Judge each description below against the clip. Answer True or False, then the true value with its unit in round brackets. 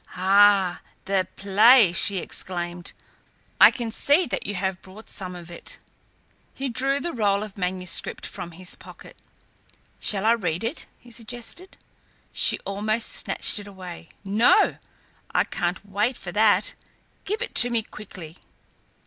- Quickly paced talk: False (145 wpm)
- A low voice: False (200 Hz)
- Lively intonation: False (3.9 semitones)